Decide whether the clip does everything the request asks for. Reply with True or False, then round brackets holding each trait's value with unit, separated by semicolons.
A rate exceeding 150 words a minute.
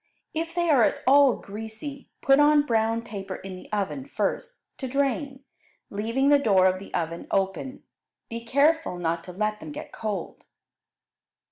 True (160 wpm)